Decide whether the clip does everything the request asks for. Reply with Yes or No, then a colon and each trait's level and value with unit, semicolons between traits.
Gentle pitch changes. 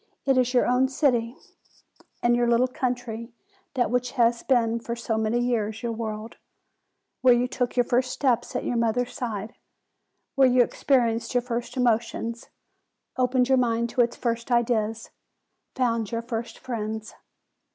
Yes: narrow, 1.5 semitones